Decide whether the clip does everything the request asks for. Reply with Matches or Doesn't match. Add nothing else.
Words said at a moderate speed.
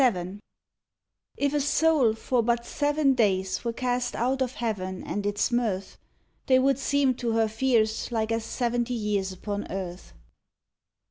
Matches